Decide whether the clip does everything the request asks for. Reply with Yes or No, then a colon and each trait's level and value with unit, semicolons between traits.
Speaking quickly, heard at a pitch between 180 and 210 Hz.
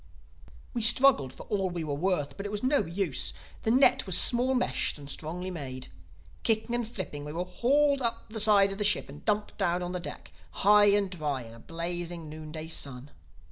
Yes: fast, 210 wpm; medium, 185 Hz